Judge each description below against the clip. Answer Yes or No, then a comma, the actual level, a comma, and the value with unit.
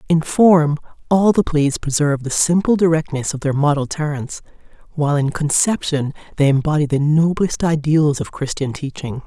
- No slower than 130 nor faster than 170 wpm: Yes, average, 155 wpm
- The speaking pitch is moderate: Yes, medium, 150 Hz